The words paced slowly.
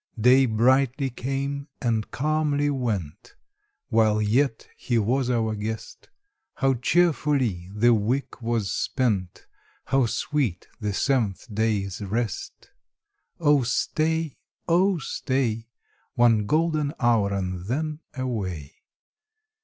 Yes: slow, 105 wpm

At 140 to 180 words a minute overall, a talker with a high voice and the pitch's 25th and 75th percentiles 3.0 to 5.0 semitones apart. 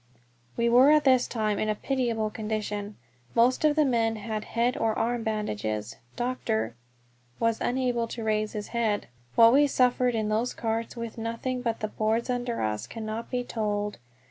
No: average, 170 wpm; high, 230 Hz; narrow, 2.4 semitones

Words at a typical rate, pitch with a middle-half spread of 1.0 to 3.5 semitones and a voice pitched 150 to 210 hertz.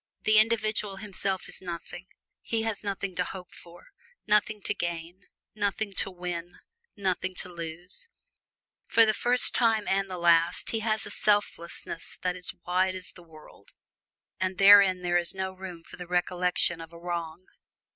Yes: average, 165 wpm; average, 2.7 semitones; medium, 185 Hz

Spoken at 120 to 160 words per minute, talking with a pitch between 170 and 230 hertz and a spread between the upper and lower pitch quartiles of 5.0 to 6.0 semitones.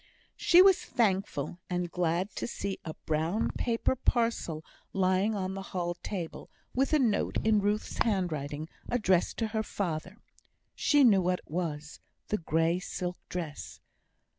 No: average, 145 wpm; medium, 185 Hz; average, 4.3 semitones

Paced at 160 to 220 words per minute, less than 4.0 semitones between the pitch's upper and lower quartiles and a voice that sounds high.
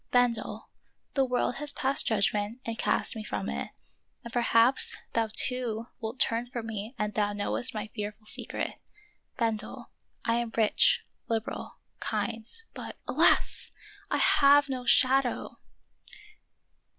No: average, 140 wpm; average, 2.7 semitones; high, 230 Hz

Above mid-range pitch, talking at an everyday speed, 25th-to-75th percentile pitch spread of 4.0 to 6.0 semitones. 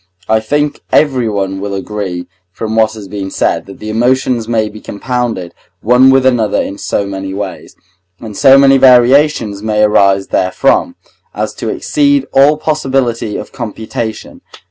No: low, 110 Hz; average, 150 wpm; average, 4.5 semitones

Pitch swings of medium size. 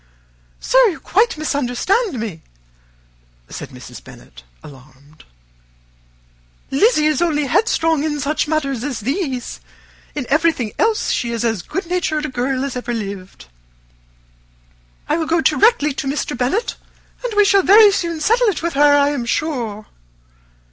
No: wide, 5.8 semitones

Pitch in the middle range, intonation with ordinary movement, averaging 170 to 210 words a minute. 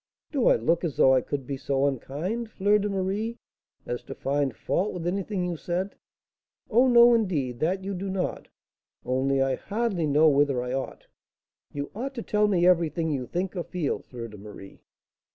No: medium, 170 Hz; wide, 6.6 semitones; average, 190 wpm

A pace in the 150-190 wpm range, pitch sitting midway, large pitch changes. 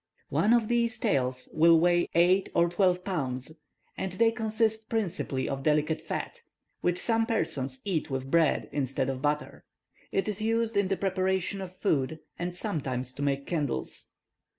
Yes: average, 160 wpm; medium, 175 Hz; wide, 6.3 semitones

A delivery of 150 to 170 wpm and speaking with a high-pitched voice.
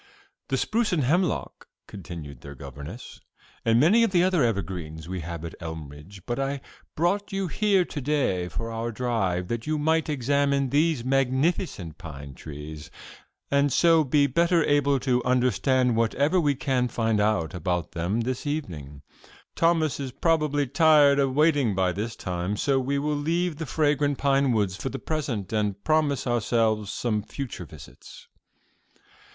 No: average, 155 wpm; low, 125 Hz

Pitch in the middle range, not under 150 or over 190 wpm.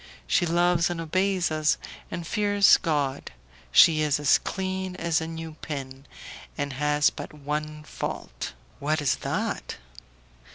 No: medium, 155 Hz; slow, 135 wpm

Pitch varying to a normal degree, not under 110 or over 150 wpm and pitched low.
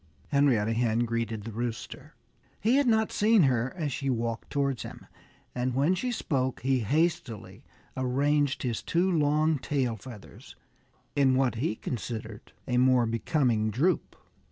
Yes: average, 4.3 semitones; average, 145 wpm; low, 130 Hz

